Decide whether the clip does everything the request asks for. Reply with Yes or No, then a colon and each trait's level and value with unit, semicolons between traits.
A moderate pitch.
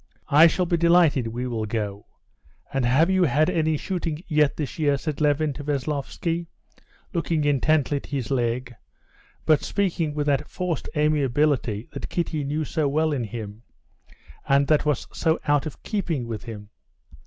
Yes: medium, 145 Hz